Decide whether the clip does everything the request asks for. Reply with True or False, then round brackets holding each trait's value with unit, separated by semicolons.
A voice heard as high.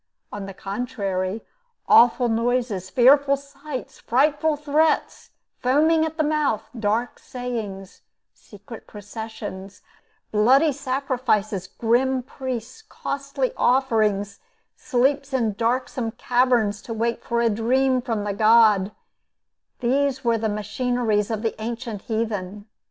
True (235 Hz)